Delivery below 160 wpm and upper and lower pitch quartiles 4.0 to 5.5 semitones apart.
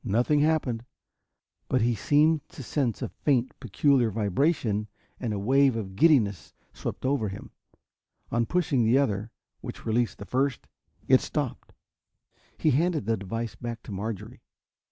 Yes: average, 145 wpm; average, 4.4 semitones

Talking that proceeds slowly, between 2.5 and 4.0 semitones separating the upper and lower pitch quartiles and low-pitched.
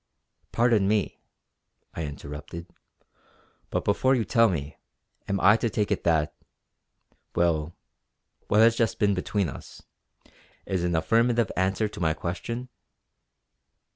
No: slow, 125 wpm; average, 5.2 semitones; low, 100 Hz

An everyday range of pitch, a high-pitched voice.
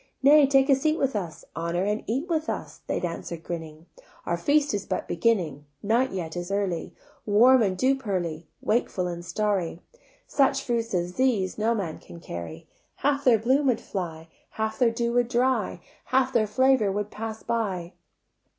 No: wide, 6.7 semitones; high, 215 Hz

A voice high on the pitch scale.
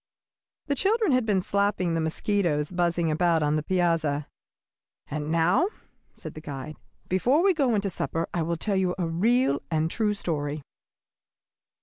No: medium, 175 Hz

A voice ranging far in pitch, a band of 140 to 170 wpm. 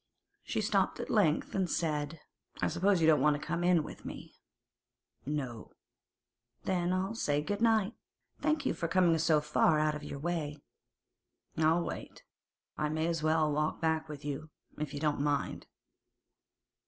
No: average, 2.7 semitones; average, 165 wpm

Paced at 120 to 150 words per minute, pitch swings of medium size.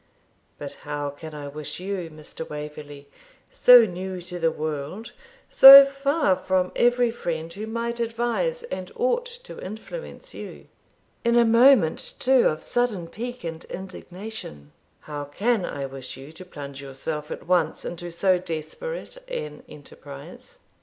No: average, 145 wpm; wide, 7.8 semitones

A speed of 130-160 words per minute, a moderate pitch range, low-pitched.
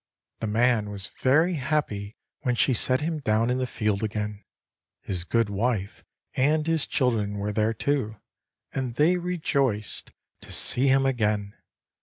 Yes: average, 150 wpm; average, 4.7 semitones; low, 120 Hz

